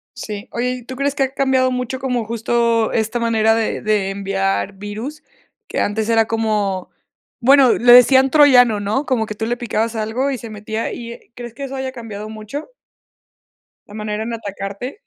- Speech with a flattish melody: No, average, 3.0 semitones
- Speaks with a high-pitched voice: Yes, high, 230 Hz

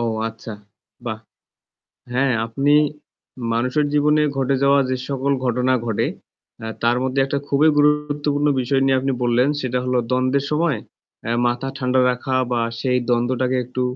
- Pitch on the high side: No, low, 130 Hz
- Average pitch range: No, narrow, 2.2 semitones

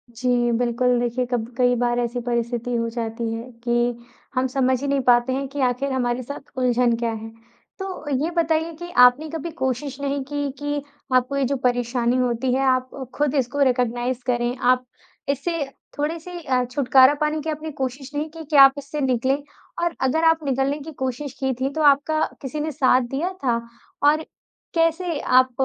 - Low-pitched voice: No, very high, 265 Hz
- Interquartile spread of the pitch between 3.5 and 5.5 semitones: No, average, 3.0 semitones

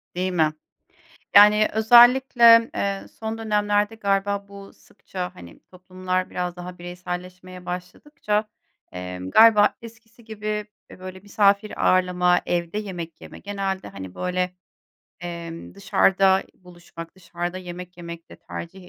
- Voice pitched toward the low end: No, medium, 185 Hz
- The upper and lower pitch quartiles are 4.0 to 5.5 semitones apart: No, average, 2.7 semitones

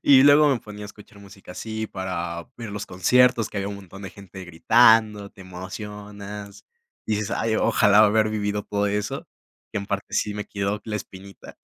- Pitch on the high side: No, low, 105 Hz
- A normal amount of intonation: No, narrow, 1.6 semitones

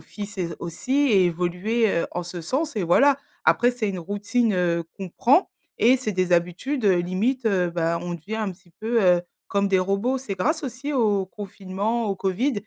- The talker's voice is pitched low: No, high, 200 Hz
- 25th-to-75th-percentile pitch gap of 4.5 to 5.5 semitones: Yes, average, 5.1 semitones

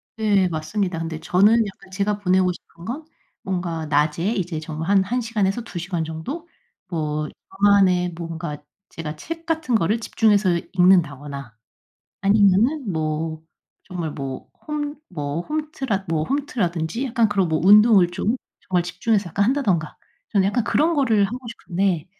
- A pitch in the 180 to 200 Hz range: Yes, high, 190 Hz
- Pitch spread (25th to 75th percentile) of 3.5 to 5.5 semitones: Yes, average, 5.1 semitones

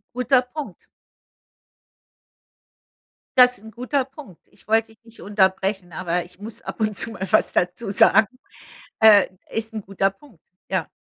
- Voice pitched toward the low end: No, high, 215 Hz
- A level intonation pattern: No, average, 3.6 semitones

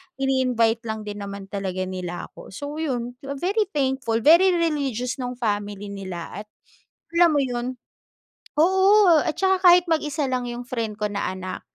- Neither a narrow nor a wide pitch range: No, wide, 6.8 semitones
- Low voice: No, high, 245 Hz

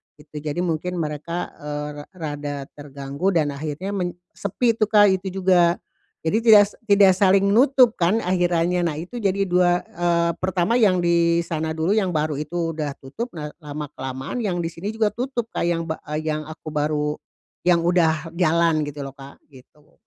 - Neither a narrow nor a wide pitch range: Yes, average, 3.9 semitones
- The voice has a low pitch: No, medium, 170 Hz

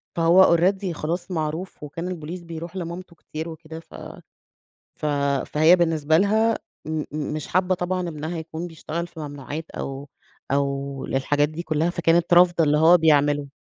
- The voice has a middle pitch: Yes, medium, 165 Hz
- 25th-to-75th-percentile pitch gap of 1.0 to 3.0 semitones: Yes, narrow, 2.4 semitones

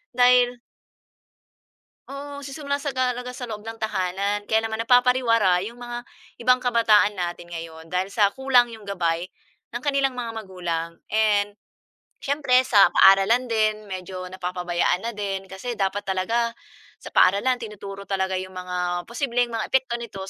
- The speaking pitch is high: Yes, high, 220 Hz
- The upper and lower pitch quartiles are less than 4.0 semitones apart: No, average, 4.5 semitones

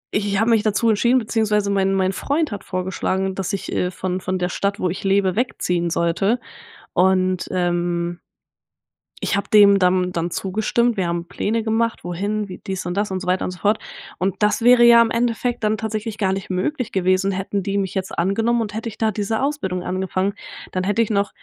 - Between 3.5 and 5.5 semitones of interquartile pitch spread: No, average, 2.9 semitones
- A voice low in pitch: No, high, 195 Hz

